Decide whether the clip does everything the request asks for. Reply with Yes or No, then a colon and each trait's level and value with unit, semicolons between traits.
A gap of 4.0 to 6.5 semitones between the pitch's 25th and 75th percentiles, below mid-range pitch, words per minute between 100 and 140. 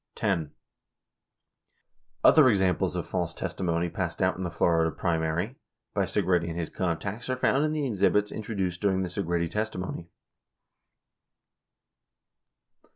No: average, 3.4 semitones; very low, 90 Hz; slow, 135 wpm